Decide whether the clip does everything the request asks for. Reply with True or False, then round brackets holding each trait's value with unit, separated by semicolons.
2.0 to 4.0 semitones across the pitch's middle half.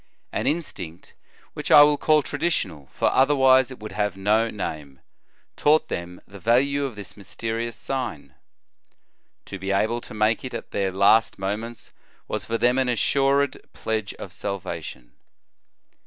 False (5.2 semitones)